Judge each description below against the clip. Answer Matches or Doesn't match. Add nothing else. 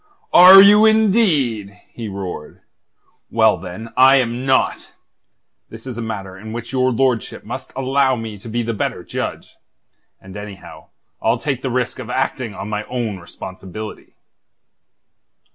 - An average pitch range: Matches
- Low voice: Matches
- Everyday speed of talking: Matches